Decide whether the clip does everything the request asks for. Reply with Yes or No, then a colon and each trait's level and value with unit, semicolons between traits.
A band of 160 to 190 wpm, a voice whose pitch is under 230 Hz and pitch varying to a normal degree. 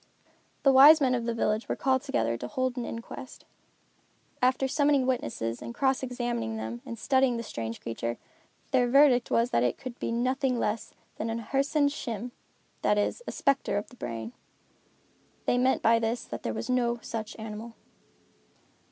No: average, 175 wpm; high, 240 Hz; average, 3.5 semitones